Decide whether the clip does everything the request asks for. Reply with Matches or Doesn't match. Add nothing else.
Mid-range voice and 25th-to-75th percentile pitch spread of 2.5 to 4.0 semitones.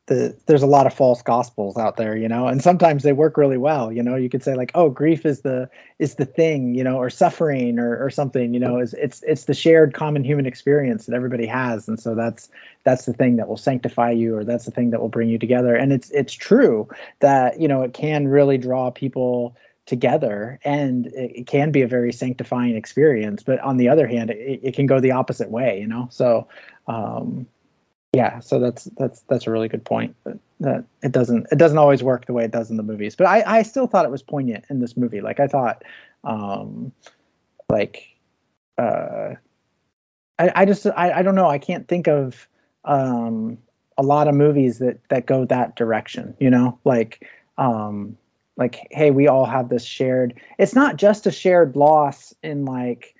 Doesn't match